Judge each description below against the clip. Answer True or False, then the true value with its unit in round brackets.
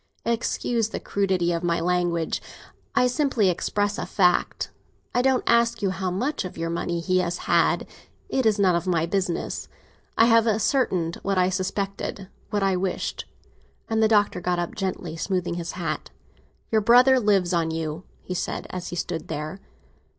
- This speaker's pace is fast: False (170 wpm)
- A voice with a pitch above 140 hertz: True (185 Hz)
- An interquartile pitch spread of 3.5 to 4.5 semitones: True (3.9 semitones)